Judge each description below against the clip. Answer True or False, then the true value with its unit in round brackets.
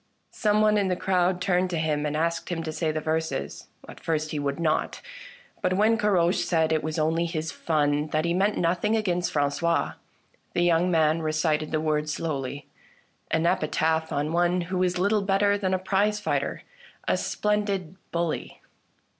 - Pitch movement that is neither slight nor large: True (3.1 semitones)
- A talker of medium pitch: True (170 Hz)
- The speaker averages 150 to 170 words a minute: False (185 wpm)